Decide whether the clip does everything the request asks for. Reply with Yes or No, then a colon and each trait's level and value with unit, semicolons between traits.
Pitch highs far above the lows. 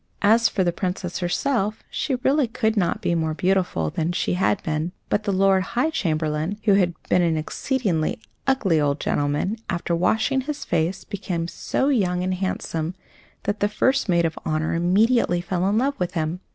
No: average, 4.3 semitones